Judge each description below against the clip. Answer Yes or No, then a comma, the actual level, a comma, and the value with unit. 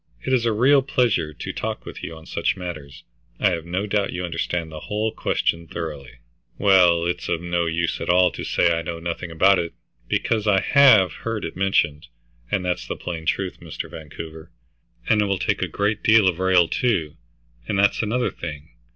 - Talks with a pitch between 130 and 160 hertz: No, very low, 90 Hz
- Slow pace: No, average, 195 wpm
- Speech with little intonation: No, average, 3.7 semitones